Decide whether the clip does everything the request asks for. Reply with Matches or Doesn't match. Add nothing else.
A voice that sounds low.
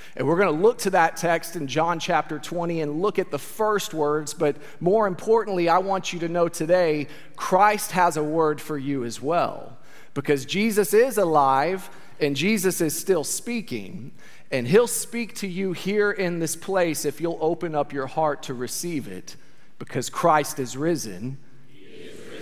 Doesn't match